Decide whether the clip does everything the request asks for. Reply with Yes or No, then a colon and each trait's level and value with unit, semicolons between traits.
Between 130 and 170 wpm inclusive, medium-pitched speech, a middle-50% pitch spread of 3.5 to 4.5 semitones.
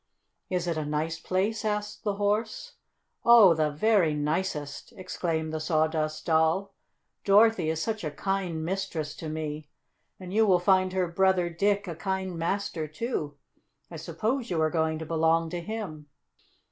Yes: average, 160 wpm; medium, 175 Hz; average, 3.9 semitones